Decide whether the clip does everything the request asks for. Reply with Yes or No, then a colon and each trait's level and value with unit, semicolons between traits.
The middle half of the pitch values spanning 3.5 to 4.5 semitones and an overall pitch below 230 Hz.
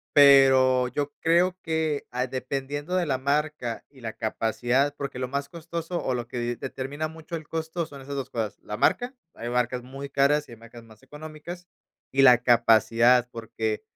Yes: average, 3.8 semitones; low, 135 Hz